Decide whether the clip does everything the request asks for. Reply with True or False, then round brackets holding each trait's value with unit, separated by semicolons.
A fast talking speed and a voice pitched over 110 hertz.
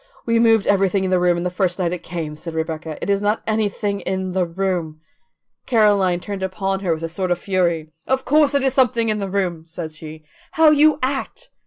True (215 wpm; 190 Hz)